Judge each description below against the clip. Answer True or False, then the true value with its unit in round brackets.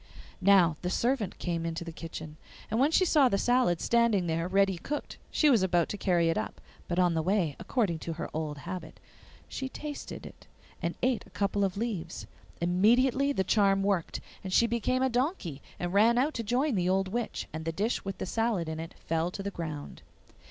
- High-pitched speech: True (195 Hz)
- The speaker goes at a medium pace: False (210 wpm)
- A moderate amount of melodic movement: False (5.7 semitones)